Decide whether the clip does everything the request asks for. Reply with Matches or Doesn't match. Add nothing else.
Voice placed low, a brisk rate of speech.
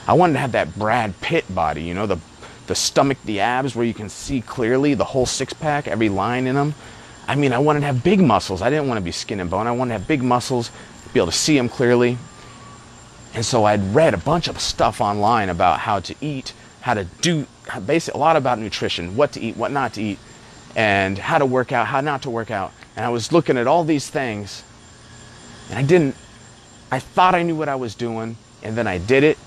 Matches